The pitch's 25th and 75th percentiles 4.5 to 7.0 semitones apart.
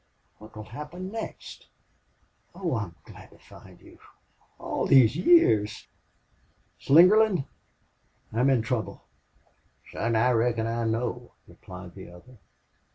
Yes: average, 5.2 semitones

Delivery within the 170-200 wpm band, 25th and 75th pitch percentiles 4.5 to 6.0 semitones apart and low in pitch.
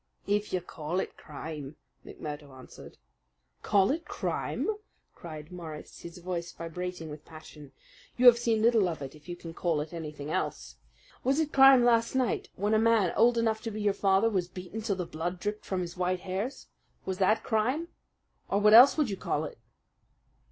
No: average, 185 wpm; average, 5.3 semitones; medium, 185 Hz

